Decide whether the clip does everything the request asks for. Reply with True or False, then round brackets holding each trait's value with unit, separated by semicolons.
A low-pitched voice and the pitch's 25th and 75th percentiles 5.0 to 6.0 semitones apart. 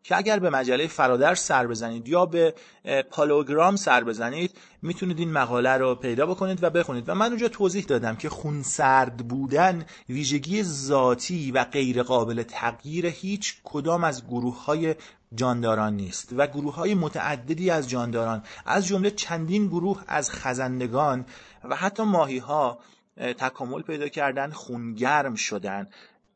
False (145 Hz; 5.6 semitones)